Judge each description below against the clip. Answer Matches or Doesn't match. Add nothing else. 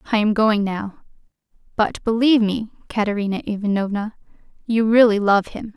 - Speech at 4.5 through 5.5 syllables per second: Matches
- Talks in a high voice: Matches